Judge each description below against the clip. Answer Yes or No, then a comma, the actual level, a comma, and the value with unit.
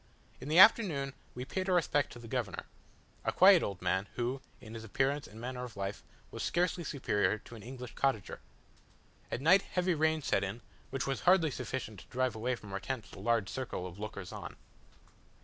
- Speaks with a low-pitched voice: Yes, low, 125 Hz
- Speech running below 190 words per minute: No, average, 200 wpm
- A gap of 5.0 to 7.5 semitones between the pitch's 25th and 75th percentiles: Yes, wide, 5.5 semitones